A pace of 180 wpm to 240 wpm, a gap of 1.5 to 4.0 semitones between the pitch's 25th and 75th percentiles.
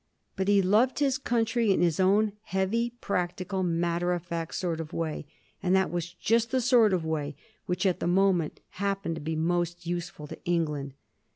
Yes: average, 190 wpm; average, 3.2 semitones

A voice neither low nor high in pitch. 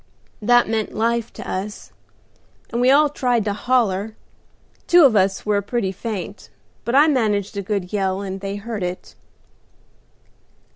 No: high, 210 Hz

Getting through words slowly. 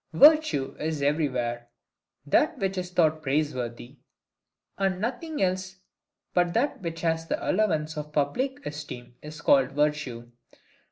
Yes: slow, 125 wpm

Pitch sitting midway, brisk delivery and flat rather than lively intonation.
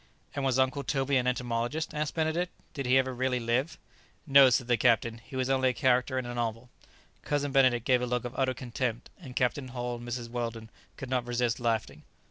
No: low, 125 Hz; fast, 210 wpm; narrow, 1.9 semitones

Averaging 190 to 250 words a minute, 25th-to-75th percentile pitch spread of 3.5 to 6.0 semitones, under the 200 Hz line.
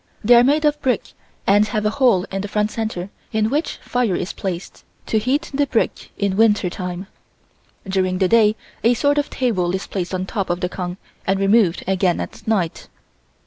No: average, 195 wpm; average, 4.0 semitones; high, 205 Hz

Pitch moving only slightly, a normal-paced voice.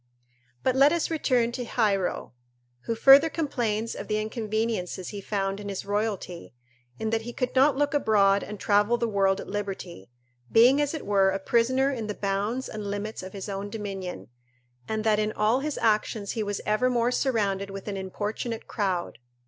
No: average, 3.3 semitones; average, 180 wpm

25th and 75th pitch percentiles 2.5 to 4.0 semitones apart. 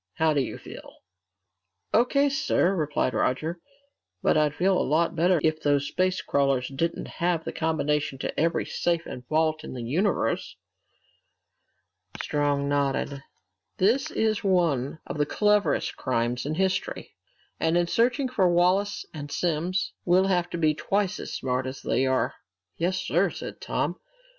No: average, 4.6 semitones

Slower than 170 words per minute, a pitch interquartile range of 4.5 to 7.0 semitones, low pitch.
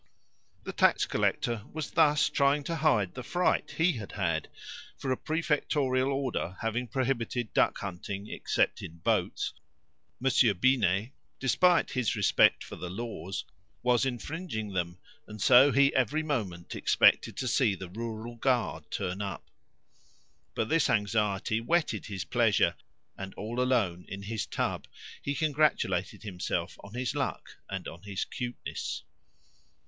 Yes: average, 140 wpm; wide, 5.4 semitones; low, 115 Hz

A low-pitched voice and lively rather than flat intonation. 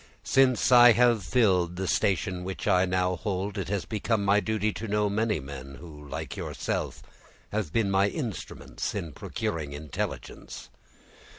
No: low, 100 Hz; average, 3.6 semitones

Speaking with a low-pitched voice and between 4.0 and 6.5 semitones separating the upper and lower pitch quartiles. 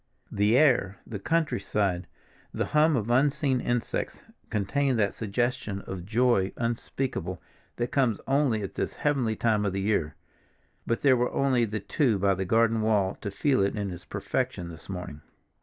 Yes: low, 110 Hz; average, 4.5 semitones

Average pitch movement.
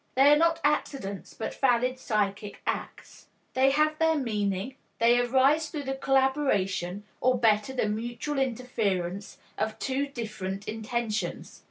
Yes: average, 4.5 semitones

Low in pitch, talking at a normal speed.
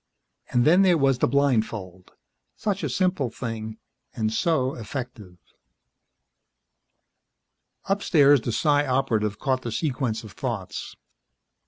No: low, 130 Hz; slow, 115 wpm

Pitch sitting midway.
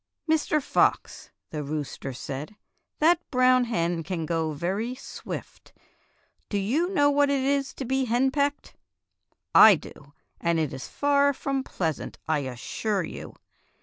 No: high, 225 Hz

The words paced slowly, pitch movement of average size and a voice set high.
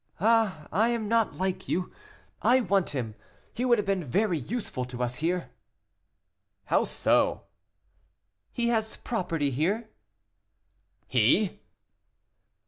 No: slow, 120 wpm; wide, 6.1 semitones; high, 195 Hz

